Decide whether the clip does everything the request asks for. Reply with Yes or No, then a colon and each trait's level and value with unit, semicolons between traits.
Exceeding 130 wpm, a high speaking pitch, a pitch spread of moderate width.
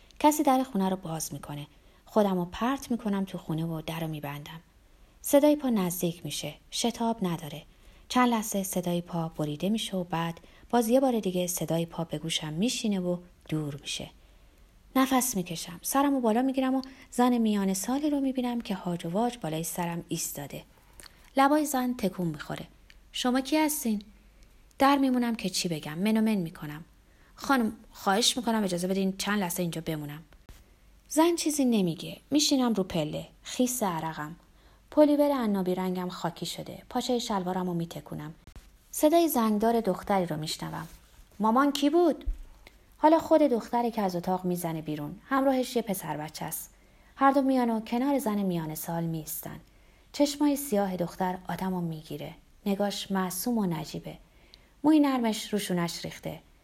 No: fast, 155 wpm; high, 195 Hz; wide, 6.8 semitones